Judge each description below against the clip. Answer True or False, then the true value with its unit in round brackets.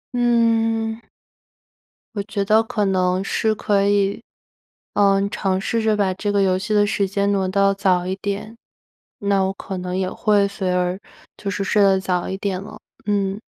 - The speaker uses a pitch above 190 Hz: True (200 Hz)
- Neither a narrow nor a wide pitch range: False (1.6 semitones)